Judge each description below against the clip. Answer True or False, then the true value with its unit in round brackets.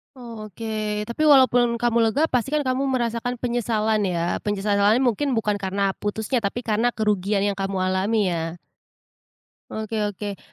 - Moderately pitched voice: False (215 Hz)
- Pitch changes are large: False (3.1 semitones)